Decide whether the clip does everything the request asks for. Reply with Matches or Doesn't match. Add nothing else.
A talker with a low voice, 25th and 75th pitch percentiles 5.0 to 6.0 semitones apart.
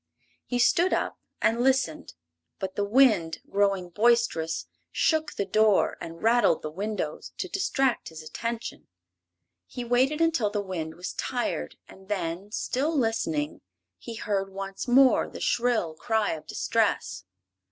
Doesn't match